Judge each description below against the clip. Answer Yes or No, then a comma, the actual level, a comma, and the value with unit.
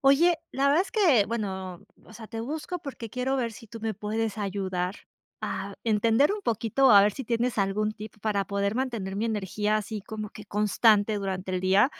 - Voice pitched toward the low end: No, high, 215 Hz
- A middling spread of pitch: Yes, average, 3.2 semitones